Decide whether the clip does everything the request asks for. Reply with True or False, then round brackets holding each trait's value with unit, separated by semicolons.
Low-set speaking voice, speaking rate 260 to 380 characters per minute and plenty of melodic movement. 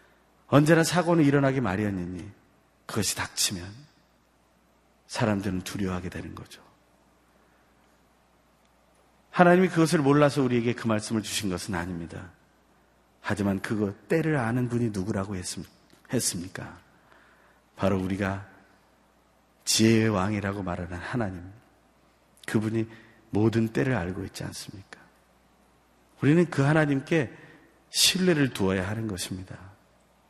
True (100 Hz; 265 characters per minute; 5.7 semitones)